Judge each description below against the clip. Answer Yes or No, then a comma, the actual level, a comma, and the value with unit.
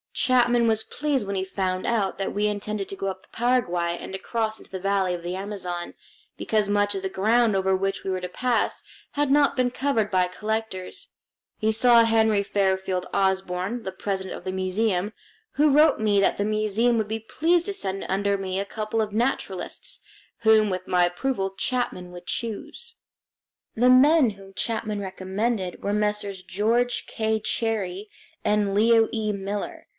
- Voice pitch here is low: No, high, 210 Hz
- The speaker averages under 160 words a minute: No, average, 175 wpm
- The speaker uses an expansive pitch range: No, average, 3.2 semitones